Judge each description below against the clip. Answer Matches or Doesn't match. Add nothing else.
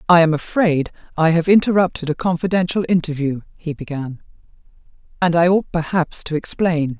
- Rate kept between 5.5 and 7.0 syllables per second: Doesn't match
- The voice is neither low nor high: Matches